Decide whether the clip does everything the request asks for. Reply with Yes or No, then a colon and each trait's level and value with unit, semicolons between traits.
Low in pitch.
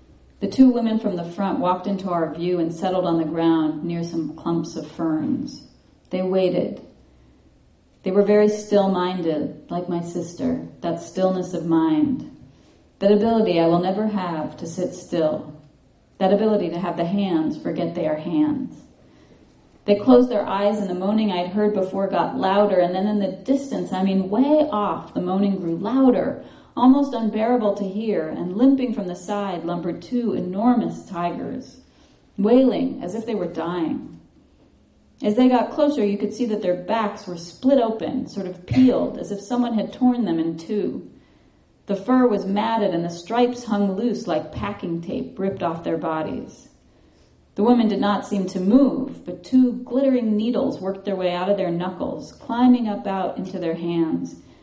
No: high, 195 Hz